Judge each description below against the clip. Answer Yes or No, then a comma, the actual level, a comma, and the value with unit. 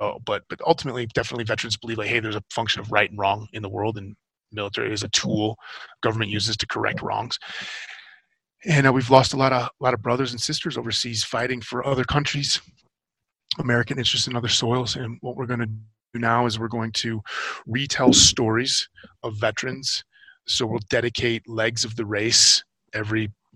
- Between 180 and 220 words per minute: Yes, average, 190 wpm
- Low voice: Yes, low, 120 Hz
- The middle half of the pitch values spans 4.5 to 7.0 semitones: No, narrow, 2.5 semitones